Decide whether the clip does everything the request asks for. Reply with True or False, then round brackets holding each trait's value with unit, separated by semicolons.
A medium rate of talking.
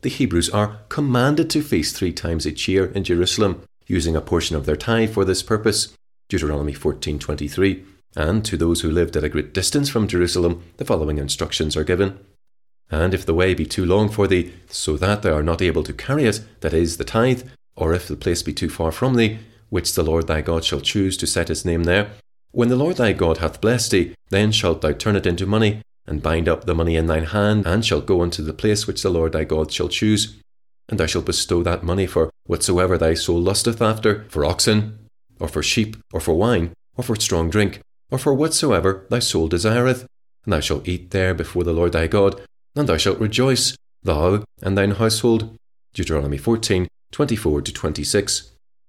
False (210 wpm)